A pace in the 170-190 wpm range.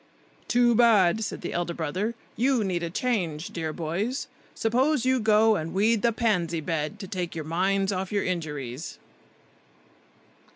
No: average, 155 wpm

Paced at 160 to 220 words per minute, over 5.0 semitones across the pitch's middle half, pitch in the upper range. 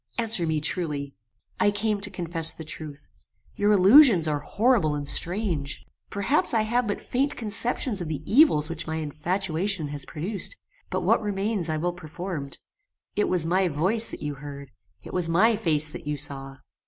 No: average, 175 wpm; wide, 5.5 semitones; medium, 175 Hz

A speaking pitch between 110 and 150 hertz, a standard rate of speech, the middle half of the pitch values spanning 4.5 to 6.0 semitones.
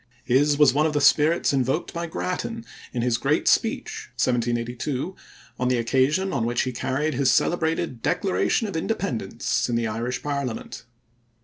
Yes: medium, 140 Hz; average, 155 wpm; average, 5.2 semitones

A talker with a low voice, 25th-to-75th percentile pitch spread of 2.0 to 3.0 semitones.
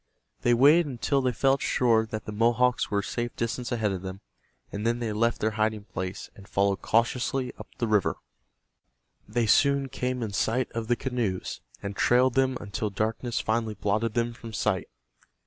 Yes: low, 115 Hz; average, 2.7 semitones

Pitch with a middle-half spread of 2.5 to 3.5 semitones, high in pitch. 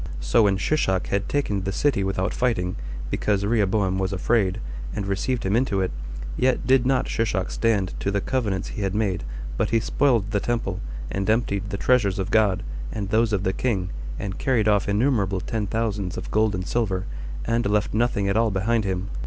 No: average, 3.0 semitones; low, 105 Hz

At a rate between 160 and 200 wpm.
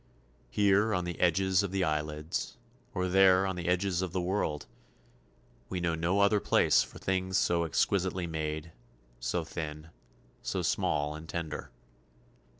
No: average, 150 wpm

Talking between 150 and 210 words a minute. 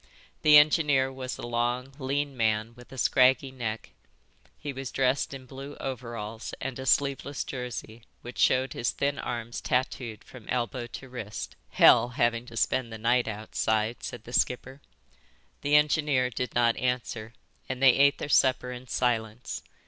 Yes: average, 160 wpm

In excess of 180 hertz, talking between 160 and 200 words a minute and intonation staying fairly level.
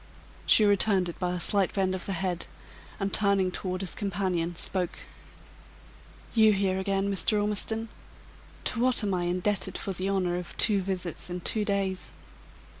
Yes: high, 190 Hz; average, 165 wpm; narrow, 1.9 semitones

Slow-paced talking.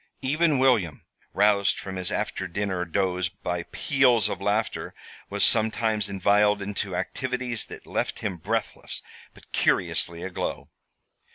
Yes: slow, 125 wpm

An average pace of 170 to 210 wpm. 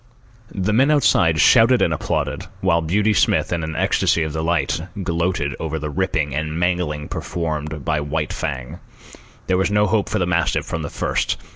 Yes: average, 175 wpm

